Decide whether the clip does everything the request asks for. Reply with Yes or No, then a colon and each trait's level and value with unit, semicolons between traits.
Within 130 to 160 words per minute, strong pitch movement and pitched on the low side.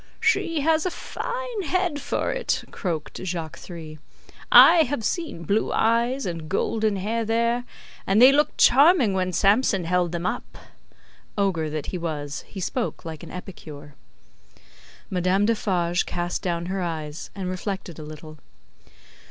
No: average, 145 wpm; wide, 6.0 semitones; high, 190 Hz